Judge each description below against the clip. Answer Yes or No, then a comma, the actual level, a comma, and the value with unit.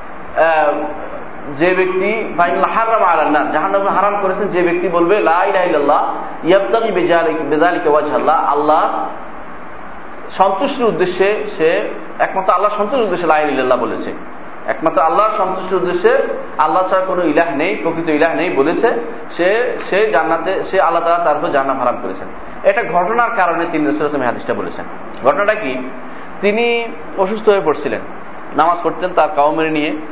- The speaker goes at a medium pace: No, fast, 130 wpm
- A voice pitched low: No, medium, 175 Hz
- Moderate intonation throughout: Yes, average, 4.1 semitones